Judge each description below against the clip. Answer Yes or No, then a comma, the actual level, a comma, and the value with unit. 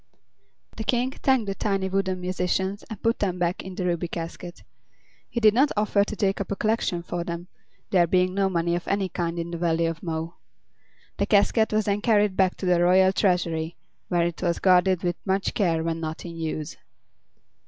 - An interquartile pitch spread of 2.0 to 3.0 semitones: Yes, average, 2.7 semitones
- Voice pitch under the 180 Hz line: No, medium, 185 Hz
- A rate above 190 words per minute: Yes, average, 200 wpm